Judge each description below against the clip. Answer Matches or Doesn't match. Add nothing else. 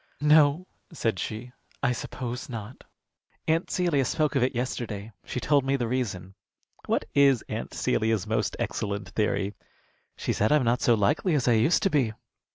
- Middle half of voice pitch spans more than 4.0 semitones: Matches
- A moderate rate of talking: Matches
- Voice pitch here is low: Matches